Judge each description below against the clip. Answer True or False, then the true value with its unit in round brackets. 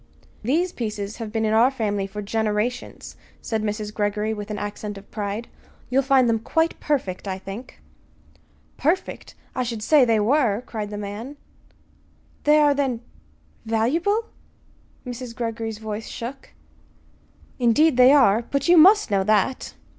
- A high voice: True (225 Hz)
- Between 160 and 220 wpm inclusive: False (145 wpm)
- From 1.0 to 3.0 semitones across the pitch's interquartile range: False (4.3 semitones)